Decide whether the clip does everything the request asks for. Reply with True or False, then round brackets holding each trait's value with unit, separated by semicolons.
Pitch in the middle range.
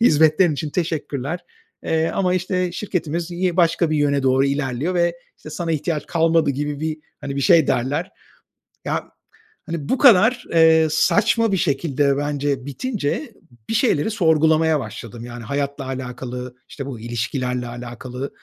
True (155 Hz)